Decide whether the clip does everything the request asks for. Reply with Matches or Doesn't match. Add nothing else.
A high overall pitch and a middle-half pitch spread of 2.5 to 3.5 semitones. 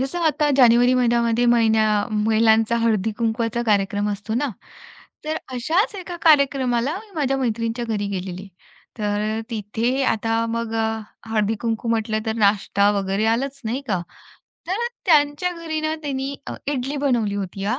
Doesn't match